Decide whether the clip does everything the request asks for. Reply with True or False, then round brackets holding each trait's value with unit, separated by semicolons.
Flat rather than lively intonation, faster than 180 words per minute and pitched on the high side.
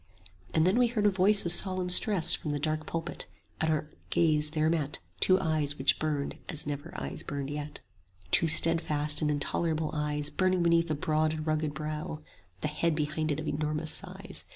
False (2.1 semitones; 200 wpm; 155 Hz)